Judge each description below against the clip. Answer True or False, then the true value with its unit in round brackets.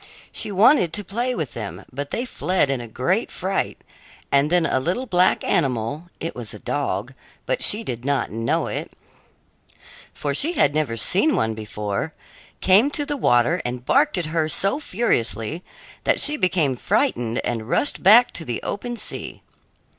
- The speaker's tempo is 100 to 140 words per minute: False (170 wpm)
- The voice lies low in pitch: False (160 Hz)